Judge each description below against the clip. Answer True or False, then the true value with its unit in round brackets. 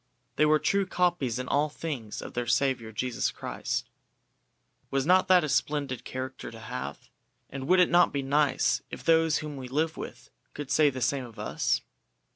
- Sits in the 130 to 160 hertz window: True (140 Hz)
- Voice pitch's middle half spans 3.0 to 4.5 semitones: True (3.7 semitones)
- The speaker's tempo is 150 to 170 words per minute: False (185 wpm)